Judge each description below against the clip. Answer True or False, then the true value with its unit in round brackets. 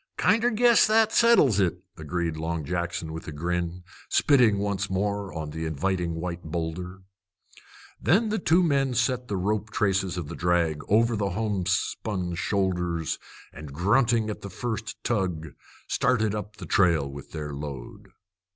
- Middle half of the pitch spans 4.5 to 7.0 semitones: True (4.8 semitones)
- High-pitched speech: False (95 Hz)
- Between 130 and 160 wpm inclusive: True (150 wpm)